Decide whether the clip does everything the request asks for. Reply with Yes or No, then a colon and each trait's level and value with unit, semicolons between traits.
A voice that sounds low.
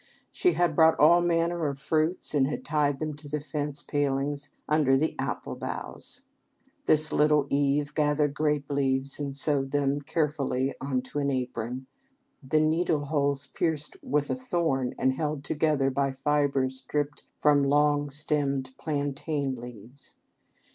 No: medium, 145 Hz